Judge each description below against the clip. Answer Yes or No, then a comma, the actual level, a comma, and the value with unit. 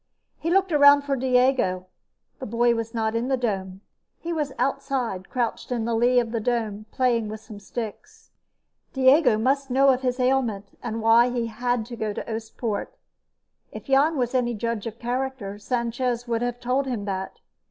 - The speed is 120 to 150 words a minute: No, average, 180 wpm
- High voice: Yes, high, 240 Hz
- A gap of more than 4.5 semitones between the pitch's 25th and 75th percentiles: No, average, 2.8 semitones